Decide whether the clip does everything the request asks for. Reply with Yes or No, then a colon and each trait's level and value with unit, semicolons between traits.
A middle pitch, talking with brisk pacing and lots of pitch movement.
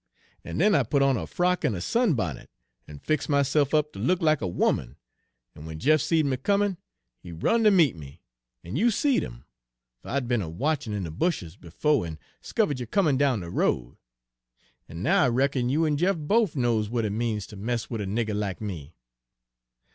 No: low, 125 Hz; fast, 215 wpm; wide, 8.0 semitones